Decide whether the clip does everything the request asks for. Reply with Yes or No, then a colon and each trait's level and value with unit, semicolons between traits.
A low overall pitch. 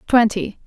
No: high, 215 Hz